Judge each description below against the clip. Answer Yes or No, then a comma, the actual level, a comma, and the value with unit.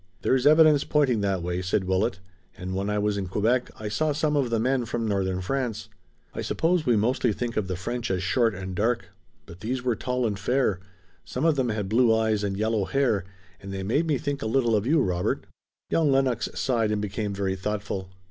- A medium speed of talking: No, fast, 215 wpm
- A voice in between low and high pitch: No, low, 110 Hz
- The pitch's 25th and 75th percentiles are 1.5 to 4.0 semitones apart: No, average, 4.6 semitones